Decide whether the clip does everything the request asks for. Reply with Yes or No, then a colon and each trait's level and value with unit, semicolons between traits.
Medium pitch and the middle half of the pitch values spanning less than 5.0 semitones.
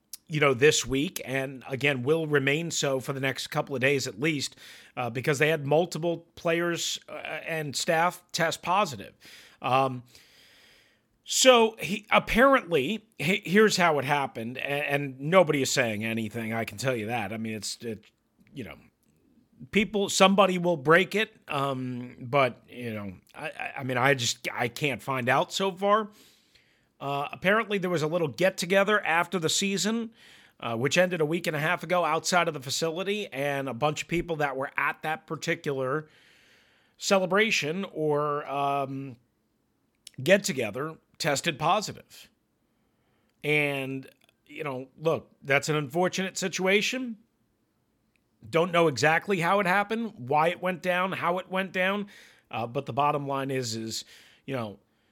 No: medium, 150 Hz; average, 5.3 semitones